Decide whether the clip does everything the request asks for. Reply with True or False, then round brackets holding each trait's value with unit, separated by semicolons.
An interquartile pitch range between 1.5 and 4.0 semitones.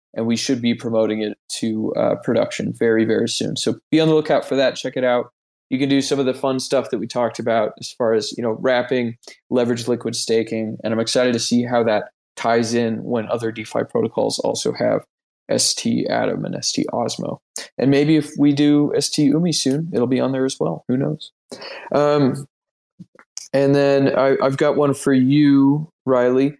True (3.3 semitones)